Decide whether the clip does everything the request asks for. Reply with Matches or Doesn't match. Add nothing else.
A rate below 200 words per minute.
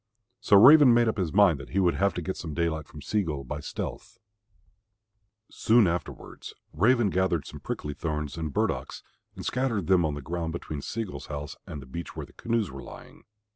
Doesn't match